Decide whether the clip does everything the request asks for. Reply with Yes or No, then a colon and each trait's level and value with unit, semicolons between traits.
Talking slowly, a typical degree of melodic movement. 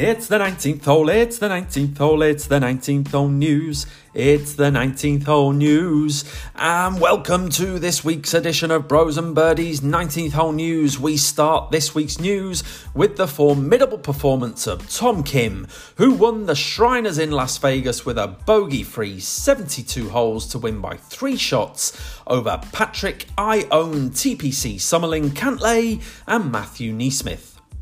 No: average, 150 wpm; average, 4.2 semitones